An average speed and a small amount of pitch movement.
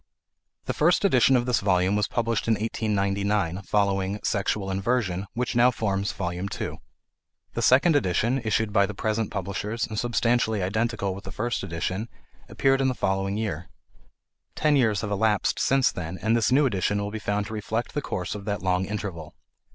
No: average, 180 wpm; average, 3.2 semitones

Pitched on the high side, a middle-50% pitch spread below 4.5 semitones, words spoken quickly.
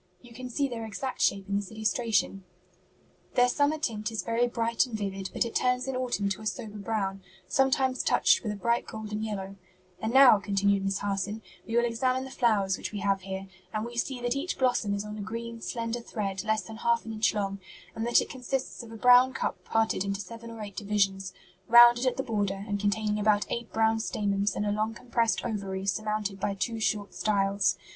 Yes: high, 220 Hz; average, 2.9 semitones; fast, 215 wpm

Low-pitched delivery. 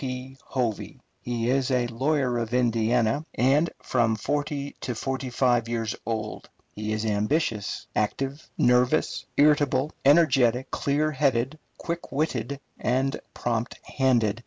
Yes: low, 125 Hz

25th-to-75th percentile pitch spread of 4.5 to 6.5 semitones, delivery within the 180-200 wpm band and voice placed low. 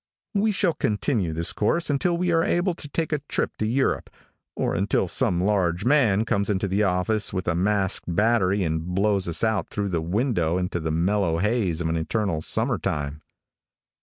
Yes: average, 5.2 semitones; average, 190 wpm; low, 100 Hz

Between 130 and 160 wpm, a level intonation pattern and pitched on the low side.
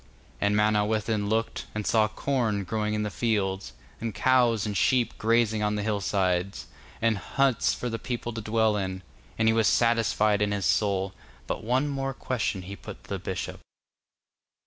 No: average, 175 wpm; narrow, 2.1 semitones; low, 110 Hz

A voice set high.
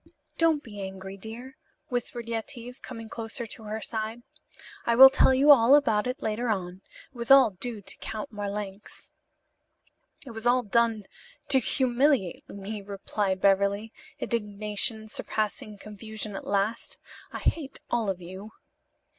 Yes: high, 220 Hz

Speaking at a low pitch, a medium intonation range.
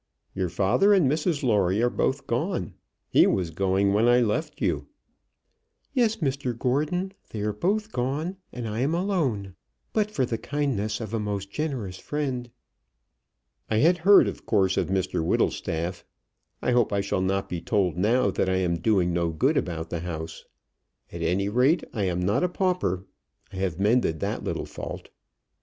No: low, 110 Hz; wide, 7.5 semitones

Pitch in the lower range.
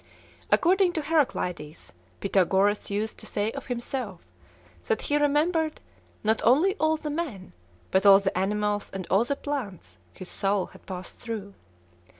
No: high, 215 Hz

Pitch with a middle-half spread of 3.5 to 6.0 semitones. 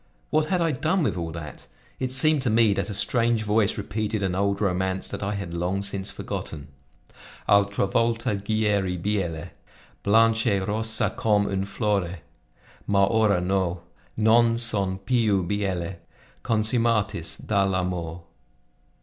No: average, 3.1 semitones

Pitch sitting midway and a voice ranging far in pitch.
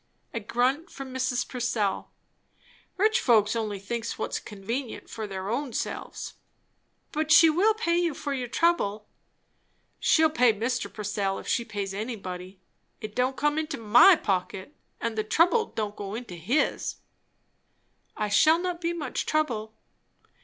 No: high, 240 Hz; wide, 6.7 semitones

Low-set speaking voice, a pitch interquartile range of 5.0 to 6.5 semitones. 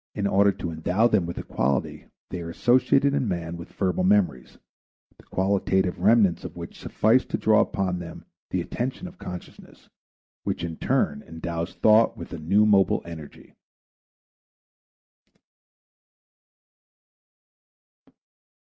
No: very low, 95 Hz; average, 4.1 semitones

